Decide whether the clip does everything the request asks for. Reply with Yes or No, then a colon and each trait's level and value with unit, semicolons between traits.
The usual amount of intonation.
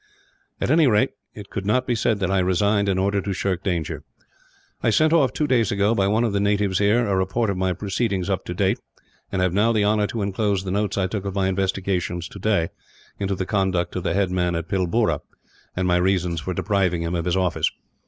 No: narrow, 2.1 semitones